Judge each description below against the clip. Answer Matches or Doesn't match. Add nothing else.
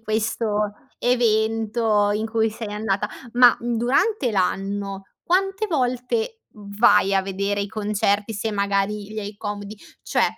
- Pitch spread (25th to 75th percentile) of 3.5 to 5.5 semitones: Doesn't match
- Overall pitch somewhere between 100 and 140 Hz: Doesn't match